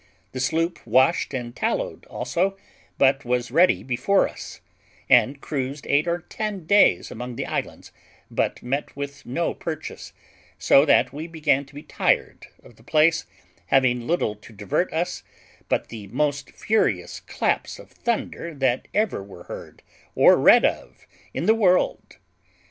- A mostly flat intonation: No, average, 5.2 semitones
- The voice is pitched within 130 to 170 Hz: Yes, medium, 140 Hz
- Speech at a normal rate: Yes, average, 150 wpm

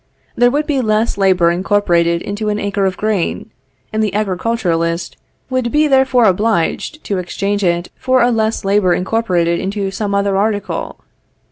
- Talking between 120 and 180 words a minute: Yes, average, 155 wpm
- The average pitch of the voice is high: Yes, high, 205 Hz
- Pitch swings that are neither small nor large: Yes, average, 3.6 semitones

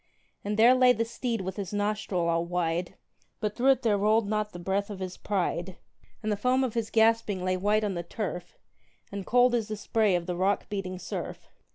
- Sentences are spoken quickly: Yes, fast, 215 wpm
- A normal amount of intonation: Yes, average, 3.5 semitones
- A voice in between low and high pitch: No, high, 205 Hz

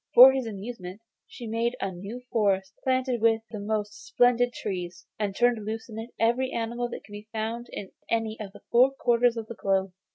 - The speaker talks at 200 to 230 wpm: Yes, fast, 205 wpm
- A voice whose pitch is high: Yes, high, 225 Hz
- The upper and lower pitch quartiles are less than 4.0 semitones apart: Yes, average, 2.8 semitones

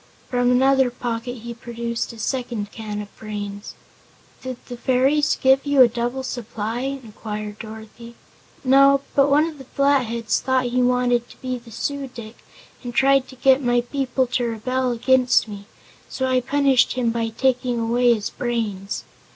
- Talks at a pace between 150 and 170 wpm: Yes, average, 165 wpm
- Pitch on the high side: Yes, high, 245 Hz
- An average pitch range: No, narrow, 2.3 semitones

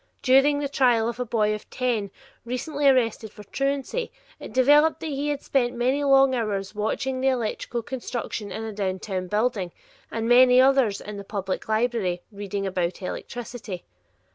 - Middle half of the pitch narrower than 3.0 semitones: No, average, 4.2 semitones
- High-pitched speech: Yes, high, 235 Hz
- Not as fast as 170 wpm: Yes, average, 160 wpm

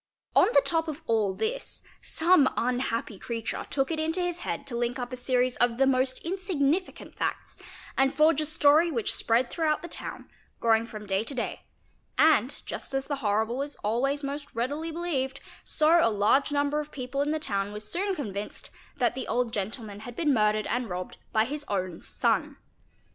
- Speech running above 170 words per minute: Yes, average, 190 wpm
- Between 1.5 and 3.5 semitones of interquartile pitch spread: No, average, 5.0 semitones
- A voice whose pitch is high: Yes, very high, 265 Hz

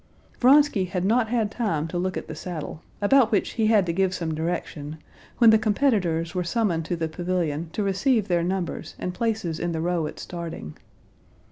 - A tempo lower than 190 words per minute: No, average, 195 wpm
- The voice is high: No, medium, 180 Hz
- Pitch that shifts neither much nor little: Yes, average, 4.6 semitones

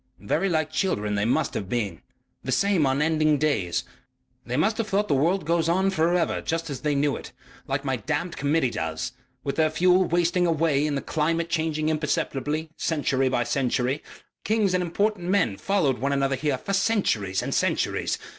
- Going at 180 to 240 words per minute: Yes, average, 185 wpm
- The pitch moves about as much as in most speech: Yes, average, 4.4 semitones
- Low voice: No, medium, 155 Hz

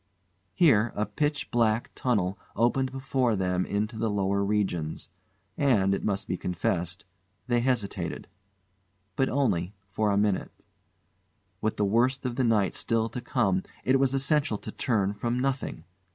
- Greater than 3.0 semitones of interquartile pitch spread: Yes, average, 4.4 semitones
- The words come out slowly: No, average, 150 wpm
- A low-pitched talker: Yes, low, 110 Hz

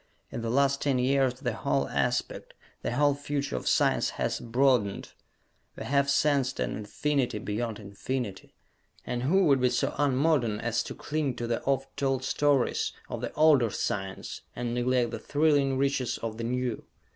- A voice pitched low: Yes, low, 130 Hz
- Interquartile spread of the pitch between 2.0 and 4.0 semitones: Yes, average, 3.1 semitones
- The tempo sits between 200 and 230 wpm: No, average, 170 wpm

